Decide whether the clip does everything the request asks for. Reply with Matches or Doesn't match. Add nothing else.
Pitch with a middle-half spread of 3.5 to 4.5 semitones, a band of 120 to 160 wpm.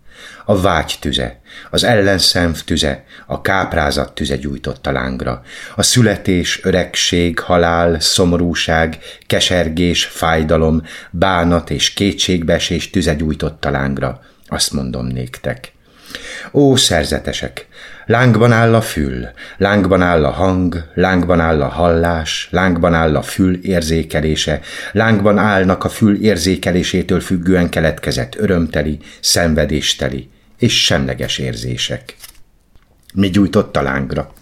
Doesn't match